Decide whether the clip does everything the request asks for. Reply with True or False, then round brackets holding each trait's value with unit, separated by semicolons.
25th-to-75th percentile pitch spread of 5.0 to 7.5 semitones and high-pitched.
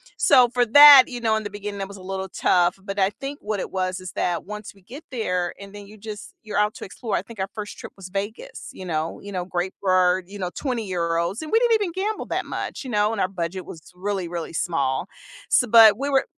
False (3.5 semitones; 200 Hz)